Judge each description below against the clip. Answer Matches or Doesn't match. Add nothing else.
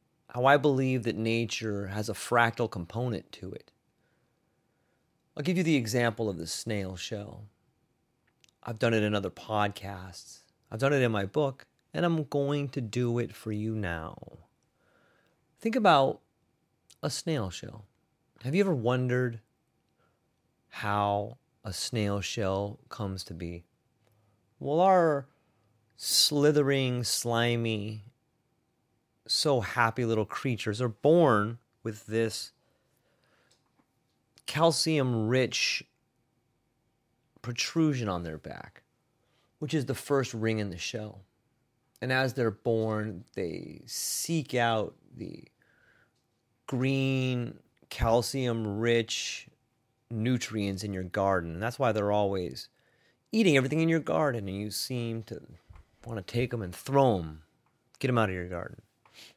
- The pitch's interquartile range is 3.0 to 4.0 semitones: Matches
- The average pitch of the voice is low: Matches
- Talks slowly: Matches